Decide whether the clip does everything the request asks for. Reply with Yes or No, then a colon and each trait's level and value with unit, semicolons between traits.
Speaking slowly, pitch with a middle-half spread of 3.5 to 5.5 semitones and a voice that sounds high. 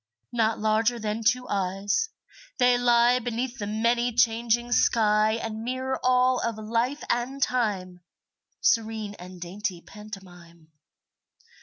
No: slow, 120 wpm; narrow, 2.6 semitones; high, 225 Hz